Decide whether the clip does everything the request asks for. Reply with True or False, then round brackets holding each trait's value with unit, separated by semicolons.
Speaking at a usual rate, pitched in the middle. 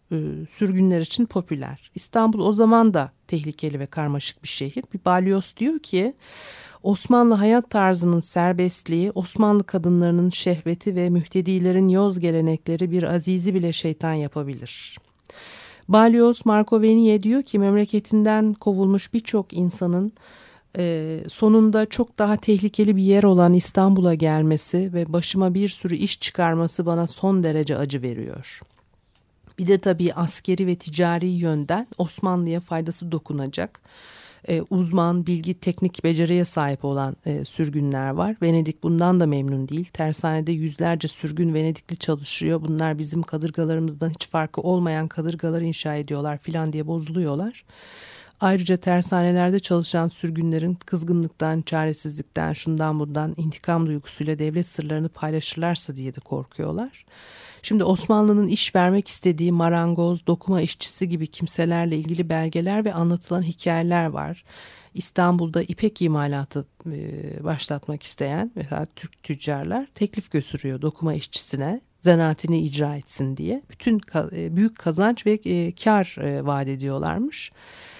True (120 wpm; 170 Hz)